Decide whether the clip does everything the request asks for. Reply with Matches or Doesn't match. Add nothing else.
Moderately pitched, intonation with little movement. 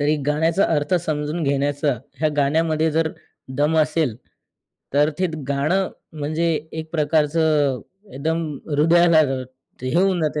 Matches